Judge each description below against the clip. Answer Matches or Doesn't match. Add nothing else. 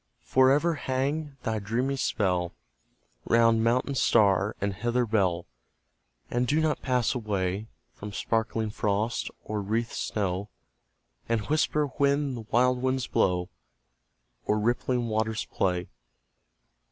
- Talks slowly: Matches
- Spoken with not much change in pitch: Doesn't match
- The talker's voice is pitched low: Matches